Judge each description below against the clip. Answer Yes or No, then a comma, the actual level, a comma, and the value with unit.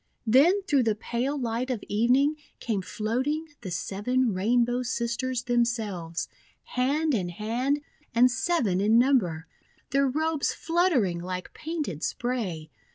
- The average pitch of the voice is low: No, high, 240 Hz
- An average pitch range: Yes, average, 4.8 semitones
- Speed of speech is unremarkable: No, slow, 125 wpm